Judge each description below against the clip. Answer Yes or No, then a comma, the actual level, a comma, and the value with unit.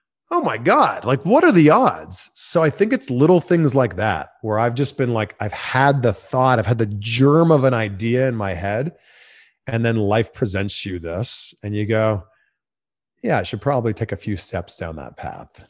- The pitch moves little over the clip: No, average, 4.3 semitones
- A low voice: Yes, low, 115 Hz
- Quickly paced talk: Yes, fast, 210 wpm